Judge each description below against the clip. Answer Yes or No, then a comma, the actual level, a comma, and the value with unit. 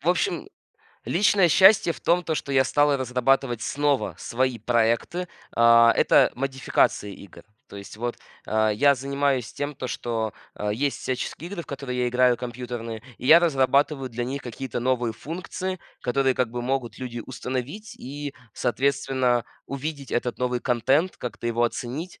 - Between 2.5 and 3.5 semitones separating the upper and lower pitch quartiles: Yes, average, 2.9 semitones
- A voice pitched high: No, low, 130 Hz